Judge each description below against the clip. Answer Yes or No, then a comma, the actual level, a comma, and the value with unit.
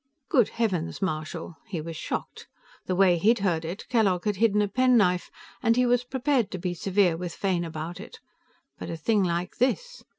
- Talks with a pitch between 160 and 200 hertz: Yes, high, 190 Hz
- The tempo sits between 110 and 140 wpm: No, average, 190 wpm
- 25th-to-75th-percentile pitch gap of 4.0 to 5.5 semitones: Yes, average, 4.9 semitones